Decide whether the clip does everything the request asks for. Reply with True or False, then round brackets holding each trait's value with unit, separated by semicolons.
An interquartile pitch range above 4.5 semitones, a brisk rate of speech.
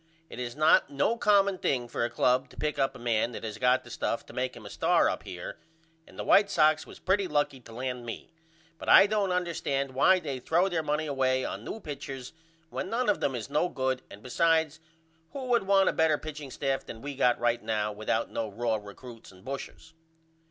True (5.1 semitones; 220 wpm)